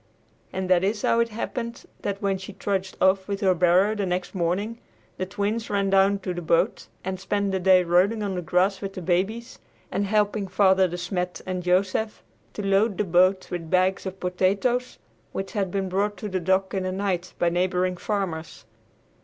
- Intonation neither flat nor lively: No, narrow, 1.8 semitones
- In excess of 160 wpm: Yes, average, 195 wpm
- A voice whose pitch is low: No, high, 190 Hz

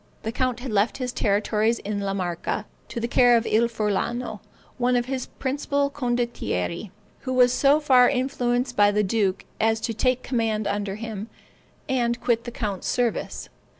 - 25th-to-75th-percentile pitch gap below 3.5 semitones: Yes, average, 3.1 semitones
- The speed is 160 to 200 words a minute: Yes, average, 170 wpm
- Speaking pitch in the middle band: No, high, 235 Hz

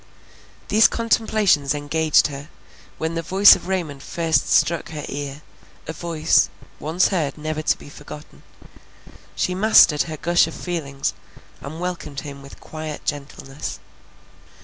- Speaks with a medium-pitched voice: Yes, medium, 155 Hz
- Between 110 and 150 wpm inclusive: Yes, slow, 135 wpm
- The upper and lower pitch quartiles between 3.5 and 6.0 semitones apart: No, average, 3.1 semitones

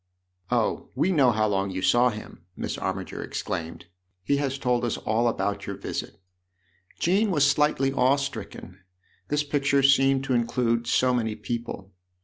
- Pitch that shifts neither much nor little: Yes, average, 4.5 semitones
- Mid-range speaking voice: No, low, 120 Hz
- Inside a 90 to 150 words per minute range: No, average, 165 wpm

